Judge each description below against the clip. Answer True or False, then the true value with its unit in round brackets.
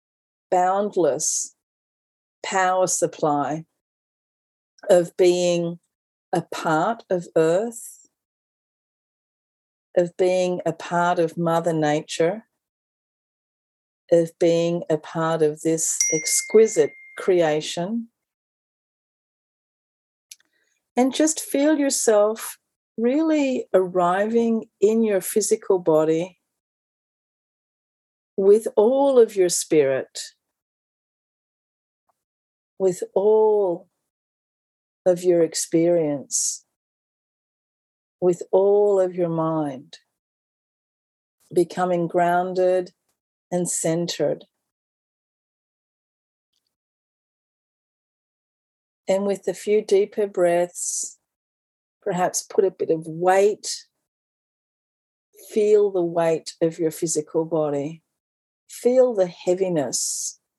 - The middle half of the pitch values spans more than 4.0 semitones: True (4.5 semitones)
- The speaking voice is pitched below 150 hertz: False (180 Hz)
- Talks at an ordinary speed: False (75 wpm)